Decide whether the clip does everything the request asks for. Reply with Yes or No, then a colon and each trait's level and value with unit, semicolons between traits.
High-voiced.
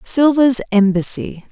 Yes: high, 235 Hz